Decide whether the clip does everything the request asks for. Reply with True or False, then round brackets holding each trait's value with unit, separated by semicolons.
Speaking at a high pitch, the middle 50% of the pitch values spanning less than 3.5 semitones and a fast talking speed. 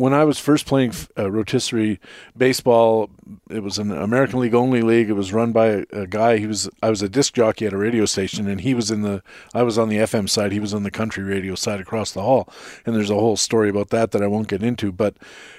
False (110 Hz; 2.4 semitones; 255 wpm)